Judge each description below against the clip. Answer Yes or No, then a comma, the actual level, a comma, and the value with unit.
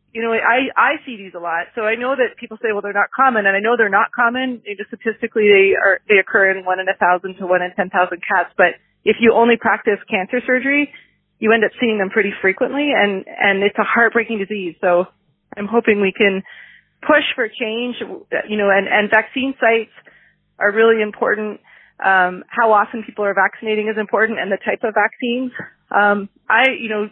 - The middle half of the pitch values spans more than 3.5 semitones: No, average, 2.9 semitones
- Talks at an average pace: No, fast, 210 wpm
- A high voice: Yes, high, 215 Hz